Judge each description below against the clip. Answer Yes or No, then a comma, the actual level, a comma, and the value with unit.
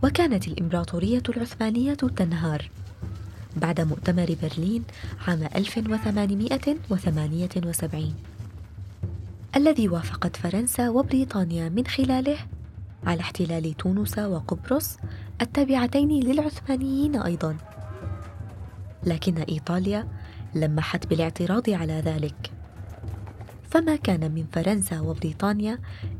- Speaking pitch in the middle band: Yes, medium, 165 Hz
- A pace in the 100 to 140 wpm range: No, average, 75 wpm